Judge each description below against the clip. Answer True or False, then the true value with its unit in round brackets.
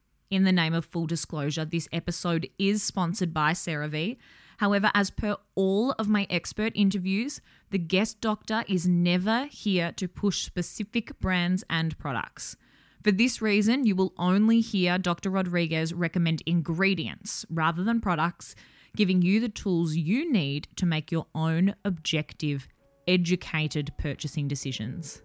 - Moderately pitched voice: True (180 Hz)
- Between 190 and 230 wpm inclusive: False (145 wpm)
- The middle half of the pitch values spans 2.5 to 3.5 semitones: False (3.9 semitones)